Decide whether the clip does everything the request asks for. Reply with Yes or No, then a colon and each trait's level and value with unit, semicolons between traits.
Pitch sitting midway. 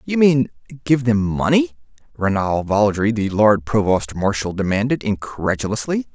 No: low, 110 Hz